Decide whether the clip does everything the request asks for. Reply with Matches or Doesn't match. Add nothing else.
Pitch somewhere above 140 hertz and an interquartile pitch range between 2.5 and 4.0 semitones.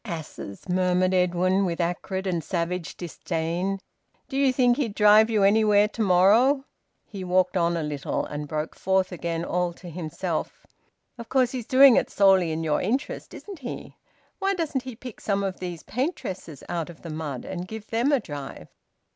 Doesn't match